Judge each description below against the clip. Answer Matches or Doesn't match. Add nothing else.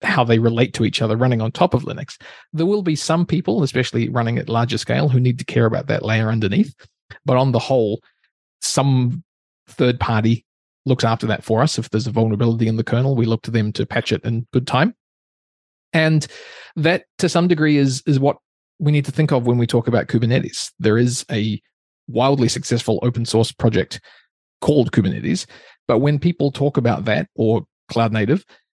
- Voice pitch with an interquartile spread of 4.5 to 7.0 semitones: Doesn't match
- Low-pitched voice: Matches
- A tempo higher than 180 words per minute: Matches